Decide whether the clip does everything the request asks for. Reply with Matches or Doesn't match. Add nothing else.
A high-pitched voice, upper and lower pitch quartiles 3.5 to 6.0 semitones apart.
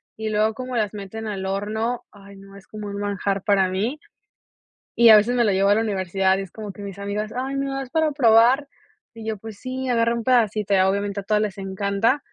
Doesn't match